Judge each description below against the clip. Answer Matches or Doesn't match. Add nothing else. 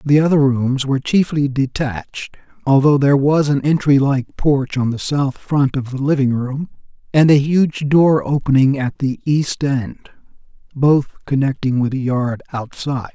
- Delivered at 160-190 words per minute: Matches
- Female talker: Doesn't match